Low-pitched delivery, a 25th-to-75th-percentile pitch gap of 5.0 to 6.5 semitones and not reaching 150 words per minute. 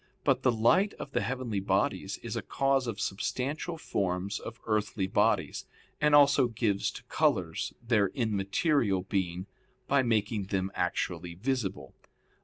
Yes: low, 110 Hz; wide, 5.5 semitones; average, 140 wpm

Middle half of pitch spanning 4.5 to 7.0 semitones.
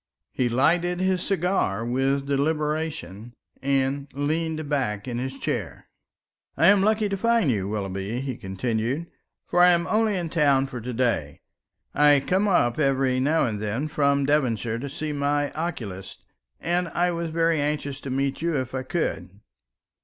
Yes: average, 5.0 semitones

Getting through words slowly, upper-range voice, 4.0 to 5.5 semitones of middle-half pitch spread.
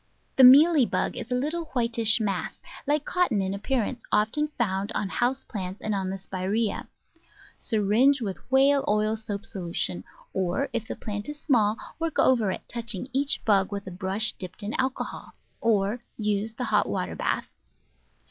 No: average, 165 wpm; high, 220 Hz; average, 4.5 semitones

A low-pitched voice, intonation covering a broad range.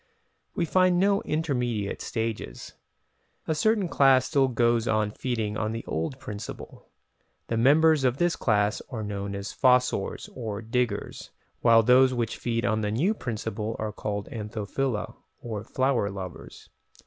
No: low, 115 Hz; average, 3.9 semitones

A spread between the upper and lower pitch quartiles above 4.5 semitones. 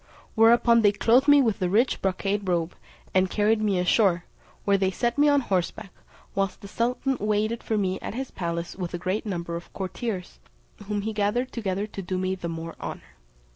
No: average, 3.6 semitones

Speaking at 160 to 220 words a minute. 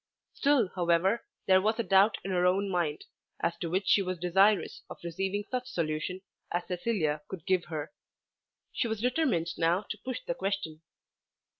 Yes: average, 170 wpm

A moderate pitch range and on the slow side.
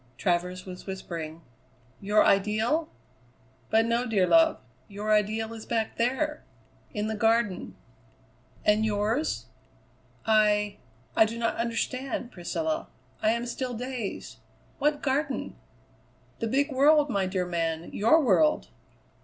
Yes: average, 4.2 semitones; slow, 120 wpm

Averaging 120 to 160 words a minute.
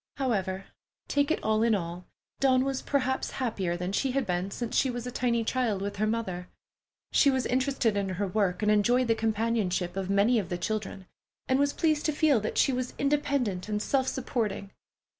No: average, 195 wpm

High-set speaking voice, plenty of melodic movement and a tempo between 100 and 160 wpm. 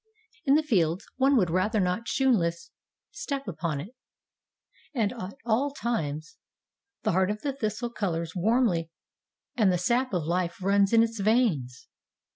Yes: high, 205 Hz; wide, 5.7 semitones; average, 150 wpm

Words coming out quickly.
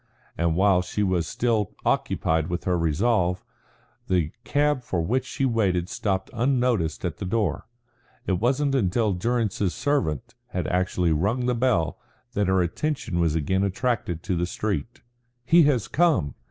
No: average, 155 wpm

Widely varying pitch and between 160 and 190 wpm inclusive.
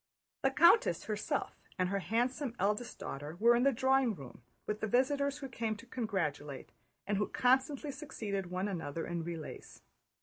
Yes: wide, 6.3 semitones; average, 165 wpm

